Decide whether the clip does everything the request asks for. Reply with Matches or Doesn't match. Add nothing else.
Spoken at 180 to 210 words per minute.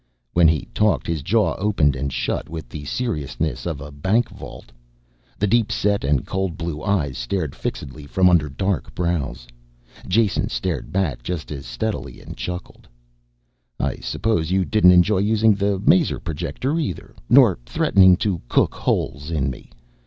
Doesn't match